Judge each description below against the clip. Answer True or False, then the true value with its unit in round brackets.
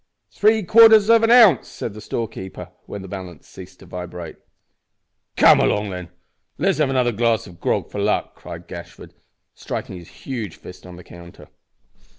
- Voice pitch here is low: True (105 Hz)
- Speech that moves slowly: False (170 wpm)